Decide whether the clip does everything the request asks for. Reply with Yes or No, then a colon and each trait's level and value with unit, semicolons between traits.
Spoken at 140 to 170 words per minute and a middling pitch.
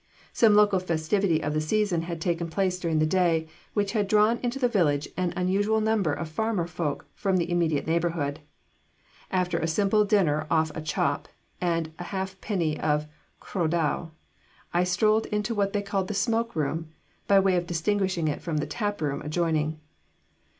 No: average, 180 wpm; medium, 175 Hz